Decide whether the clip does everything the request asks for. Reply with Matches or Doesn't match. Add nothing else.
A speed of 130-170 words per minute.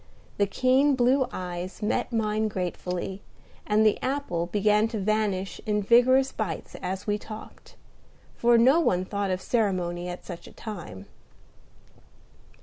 Matches